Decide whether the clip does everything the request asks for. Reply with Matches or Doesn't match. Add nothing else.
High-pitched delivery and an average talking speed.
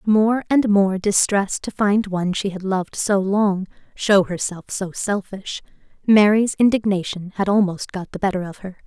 Matches